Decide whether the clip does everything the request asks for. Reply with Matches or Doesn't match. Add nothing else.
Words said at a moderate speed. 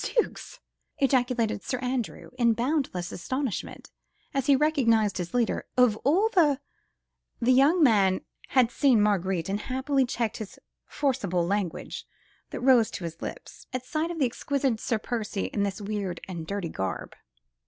Matches